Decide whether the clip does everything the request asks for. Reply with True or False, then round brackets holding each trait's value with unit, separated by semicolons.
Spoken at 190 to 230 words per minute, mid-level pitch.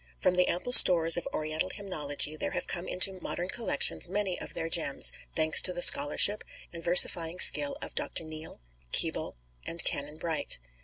False (170 wpm; 170 Hz)